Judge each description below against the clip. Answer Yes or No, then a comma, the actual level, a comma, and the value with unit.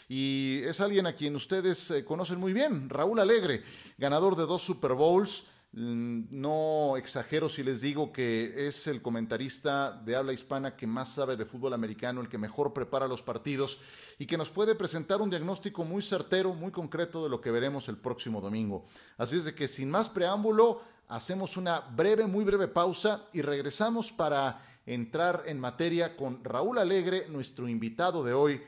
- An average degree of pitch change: No, wide, 5.8 semitones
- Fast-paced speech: No, average, 175 wpm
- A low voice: No, medium, 150 Hz